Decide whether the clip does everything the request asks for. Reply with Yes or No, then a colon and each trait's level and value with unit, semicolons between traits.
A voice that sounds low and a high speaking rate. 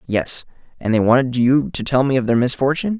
Yes: low, 130 Hz; fast, 220 wpm